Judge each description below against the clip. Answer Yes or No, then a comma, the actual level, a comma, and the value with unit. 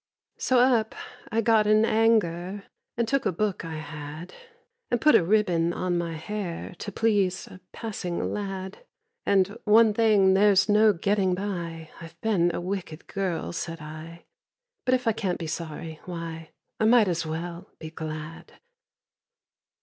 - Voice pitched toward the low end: No, medium, 185 Hz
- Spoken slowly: No, average, 155 wpm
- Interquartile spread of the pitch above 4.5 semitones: No, average, 4.2 semitones